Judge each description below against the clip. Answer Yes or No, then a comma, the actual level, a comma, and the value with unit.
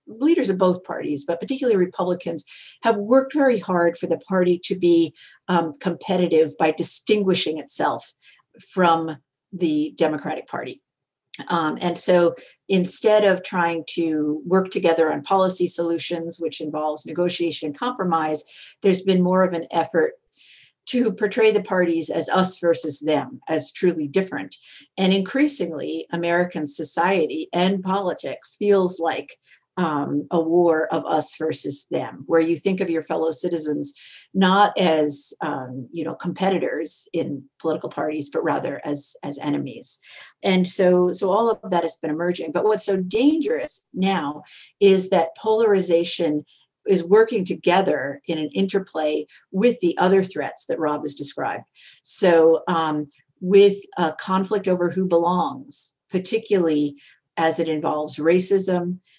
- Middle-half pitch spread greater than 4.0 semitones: No, average, 3.3 semitones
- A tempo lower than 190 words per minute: Yes, average, 140 wpm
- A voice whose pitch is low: No, medium, 175 Hz